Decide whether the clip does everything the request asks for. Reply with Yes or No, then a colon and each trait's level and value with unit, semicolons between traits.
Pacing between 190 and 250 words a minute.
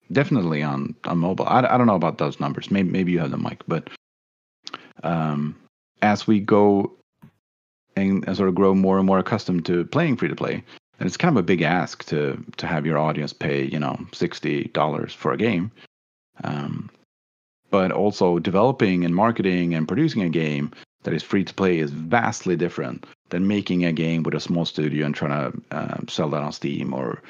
Yes: average, 200 wpm